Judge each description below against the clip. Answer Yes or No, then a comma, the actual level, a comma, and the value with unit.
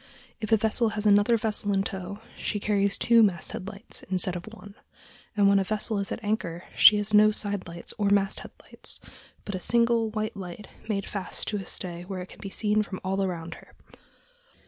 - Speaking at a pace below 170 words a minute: No, fast, 205 wpm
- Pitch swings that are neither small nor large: No, narrow, 2.0 semitones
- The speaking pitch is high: Yes, high, 205 Hz